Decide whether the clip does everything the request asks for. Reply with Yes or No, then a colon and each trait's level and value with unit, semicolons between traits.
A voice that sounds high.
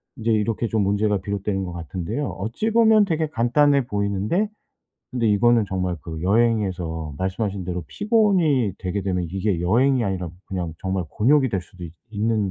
No: low, 105 Hz